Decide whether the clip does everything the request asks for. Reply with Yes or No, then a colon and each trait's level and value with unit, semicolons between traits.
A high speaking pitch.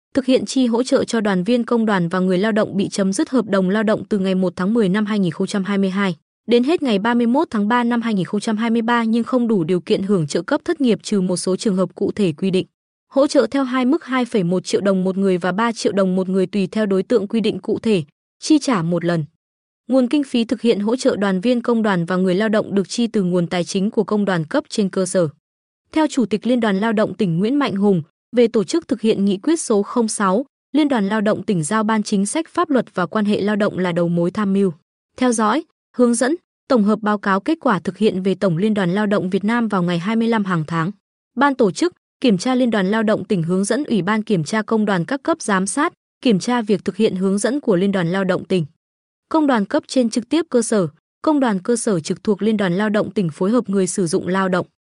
Yes: high, 215 Hz